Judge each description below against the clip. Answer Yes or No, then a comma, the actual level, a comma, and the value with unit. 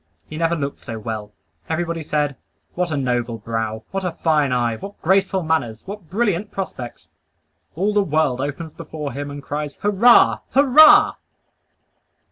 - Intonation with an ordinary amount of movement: No, wide, 6.8 semitones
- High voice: No, medium, 155 Hz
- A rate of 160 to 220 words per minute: No, average, 150 wpm